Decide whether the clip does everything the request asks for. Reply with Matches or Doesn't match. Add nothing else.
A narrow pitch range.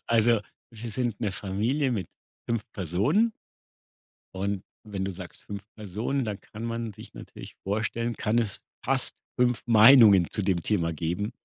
Doesn't match